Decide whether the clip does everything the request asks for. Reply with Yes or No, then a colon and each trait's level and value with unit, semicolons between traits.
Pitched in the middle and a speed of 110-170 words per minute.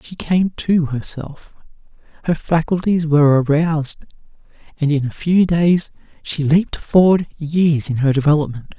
Yes: medium, 155 Hz; slow, 135 wpm